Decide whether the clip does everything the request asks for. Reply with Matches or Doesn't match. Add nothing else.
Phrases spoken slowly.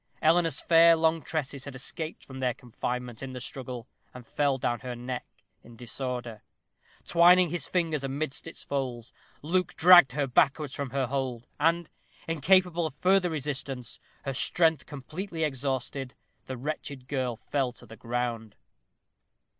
Doesn't match